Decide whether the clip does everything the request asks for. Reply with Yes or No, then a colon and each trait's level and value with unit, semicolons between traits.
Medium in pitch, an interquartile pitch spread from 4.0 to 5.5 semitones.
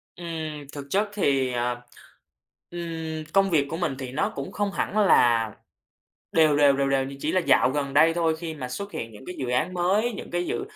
Yes: medium, 160 Hz; average, 4.5 semitones